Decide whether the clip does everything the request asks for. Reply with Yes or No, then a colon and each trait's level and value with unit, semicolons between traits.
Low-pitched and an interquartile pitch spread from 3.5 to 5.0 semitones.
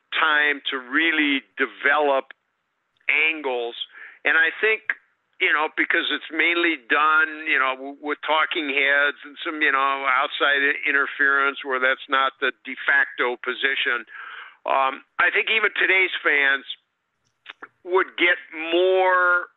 No: medium, 145 Hz; average, 4.1 semitones